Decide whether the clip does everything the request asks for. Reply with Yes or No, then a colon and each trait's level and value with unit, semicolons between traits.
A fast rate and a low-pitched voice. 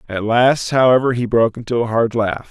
Yes: fast, 215 wpm; low, 120 Hz